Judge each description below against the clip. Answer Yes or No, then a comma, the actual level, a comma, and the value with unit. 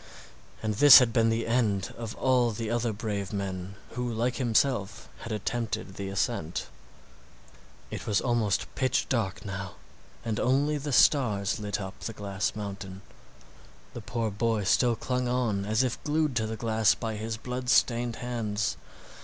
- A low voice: Yes, low, 110 Hz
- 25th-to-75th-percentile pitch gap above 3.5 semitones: No, average, 3.2 semitones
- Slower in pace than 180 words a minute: Yes, average, 160 wpm